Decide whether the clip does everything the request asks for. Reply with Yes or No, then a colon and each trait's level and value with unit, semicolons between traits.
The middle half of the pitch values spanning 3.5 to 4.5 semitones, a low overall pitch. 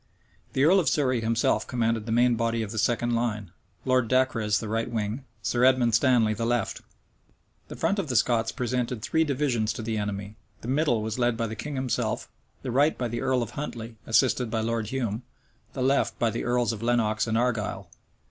No: narrow, 2.4 semitones; low, 120 Hz